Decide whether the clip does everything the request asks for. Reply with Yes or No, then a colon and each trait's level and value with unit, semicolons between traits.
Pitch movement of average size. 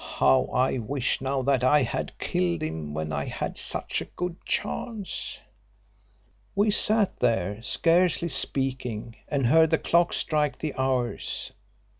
No: wide, 6.1 semitones